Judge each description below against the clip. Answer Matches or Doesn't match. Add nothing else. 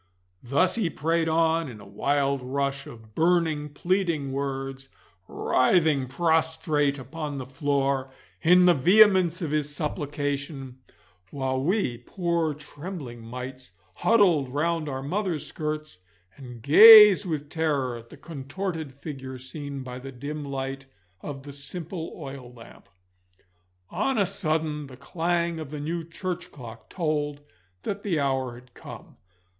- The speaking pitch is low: Doesn't match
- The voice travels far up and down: Doesn't match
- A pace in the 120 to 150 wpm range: Matches